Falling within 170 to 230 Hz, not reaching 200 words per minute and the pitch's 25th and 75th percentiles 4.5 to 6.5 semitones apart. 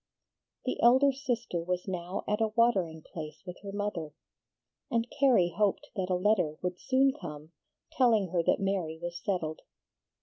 Yes: high, 190 Hz; average, 160 wpm; average, 5.0 semitones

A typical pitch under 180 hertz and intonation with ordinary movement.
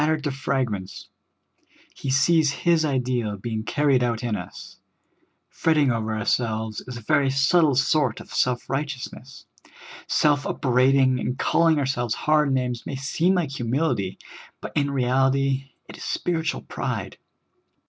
Yes: low, 135 Hz; average, 3.3 semitones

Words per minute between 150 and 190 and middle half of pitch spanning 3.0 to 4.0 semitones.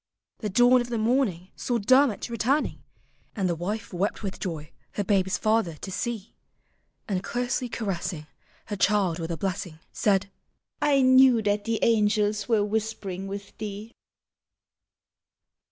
No: average, 140 wpm; average, 3.5 semitones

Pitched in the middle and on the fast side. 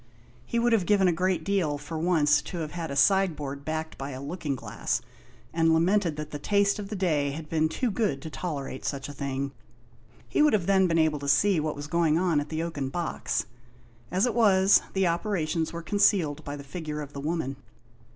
Yes: medium, 160 Hz; fast, 215 wpm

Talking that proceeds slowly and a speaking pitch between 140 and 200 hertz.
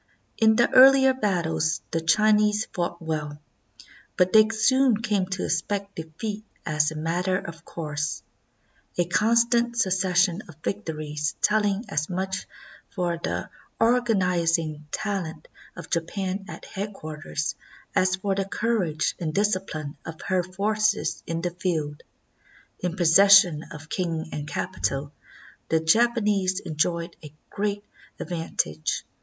Yes: slow, 130 wpm; medium, 185 Hz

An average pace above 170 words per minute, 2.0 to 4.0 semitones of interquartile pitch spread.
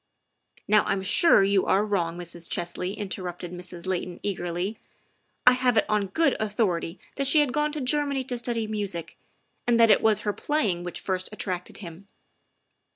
No: average, 185 wpm; average, 5.1 semitones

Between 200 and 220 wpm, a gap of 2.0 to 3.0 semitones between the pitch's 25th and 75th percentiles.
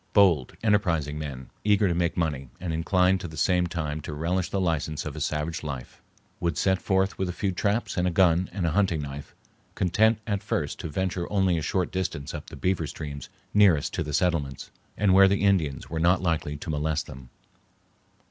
No: fast, 205 wpm; average, 4.0 semitones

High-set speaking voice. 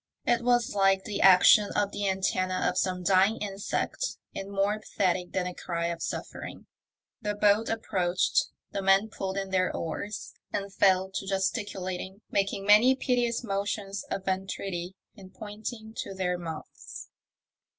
Yes: high, 195 Hz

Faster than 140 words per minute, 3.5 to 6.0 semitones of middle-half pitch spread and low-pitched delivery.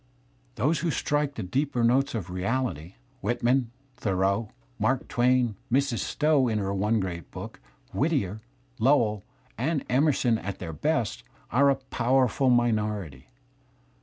Yes: average, 160 wpm; average, 5.0 semitones; low, 120 Hz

